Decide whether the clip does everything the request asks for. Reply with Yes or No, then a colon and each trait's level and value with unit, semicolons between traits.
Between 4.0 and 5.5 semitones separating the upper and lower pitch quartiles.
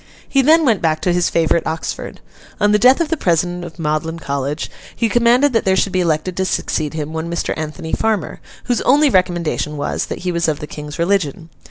Yes: average, 4.9 semitones